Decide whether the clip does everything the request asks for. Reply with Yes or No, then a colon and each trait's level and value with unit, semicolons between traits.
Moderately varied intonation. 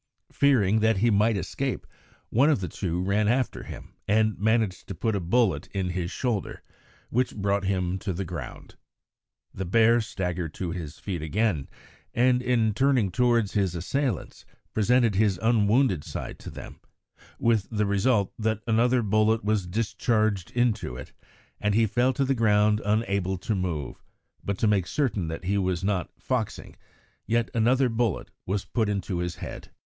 Yes: average, 3.6 semitones